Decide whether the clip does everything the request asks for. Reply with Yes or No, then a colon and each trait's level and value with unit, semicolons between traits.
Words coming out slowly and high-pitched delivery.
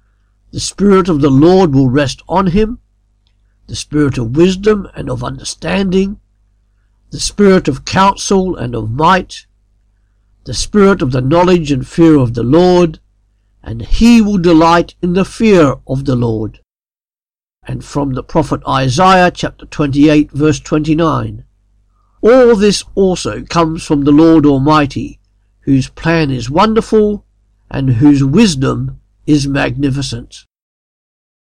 No: slow, 130 wpm; medium, 145 Hz